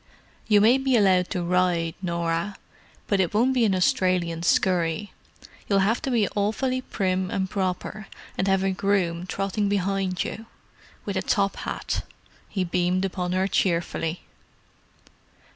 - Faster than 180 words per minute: No, average, 145 wpm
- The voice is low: No, high, 190 Hz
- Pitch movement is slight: Yes, narrow, 2.3 semitones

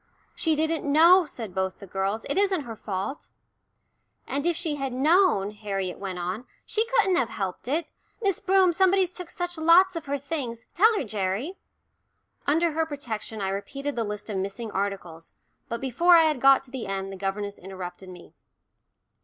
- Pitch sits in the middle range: No, very high, 265 Hz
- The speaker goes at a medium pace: Yes, average, 180 wpm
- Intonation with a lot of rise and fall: Yes, wide, 9.0 semitones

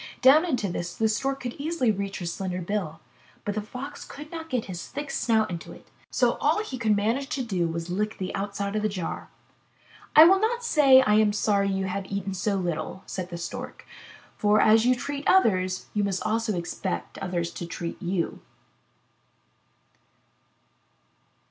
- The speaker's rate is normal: Yes, average, 180 wpm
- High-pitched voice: Yes, high, 210 Hz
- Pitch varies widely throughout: Yes, wide, 5.7 semitones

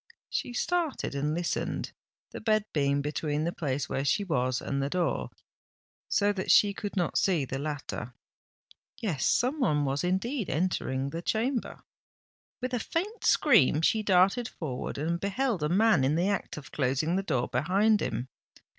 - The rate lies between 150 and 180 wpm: Yes, average, 165 wpm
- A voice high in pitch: No, medium, 175 Hz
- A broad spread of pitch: Yes, wide, 7.1 semitones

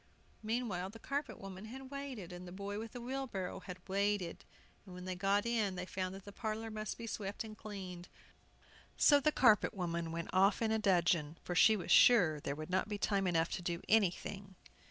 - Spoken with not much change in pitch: No, average, 3.4 semitones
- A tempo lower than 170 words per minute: No, average, 195 wpm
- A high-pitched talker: Yes, high, 195 Hz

